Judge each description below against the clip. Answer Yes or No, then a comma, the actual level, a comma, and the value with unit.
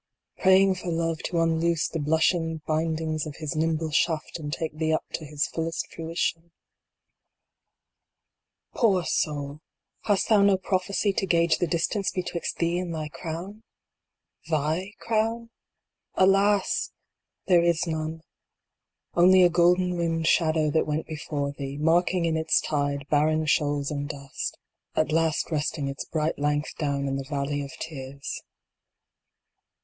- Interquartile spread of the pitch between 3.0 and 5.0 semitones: No, narrow, 2.6 semitones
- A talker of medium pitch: Yes, medium, 160 Hz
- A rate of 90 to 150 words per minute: Yes, average, 145 wpm